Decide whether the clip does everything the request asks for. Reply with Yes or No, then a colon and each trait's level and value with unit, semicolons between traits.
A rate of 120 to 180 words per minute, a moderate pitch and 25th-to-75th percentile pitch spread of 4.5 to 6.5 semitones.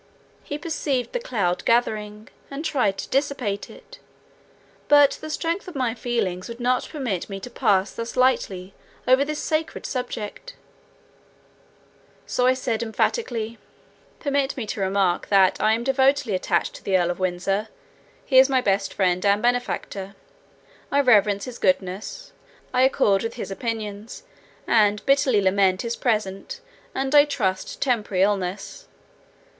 No: average, 145 wpm; high, 225 Hz; average, 5.1 semitones